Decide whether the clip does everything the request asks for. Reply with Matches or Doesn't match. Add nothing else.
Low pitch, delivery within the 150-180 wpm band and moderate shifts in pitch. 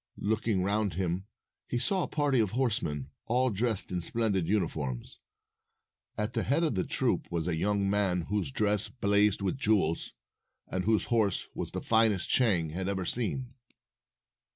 Matches